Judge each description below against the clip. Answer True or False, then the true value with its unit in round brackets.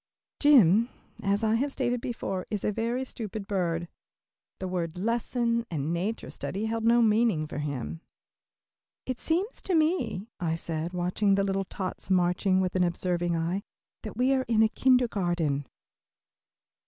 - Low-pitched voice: False (200 Hz)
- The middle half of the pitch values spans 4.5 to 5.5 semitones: True (5.0 semitones)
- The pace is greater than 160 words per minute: False (155 wpm)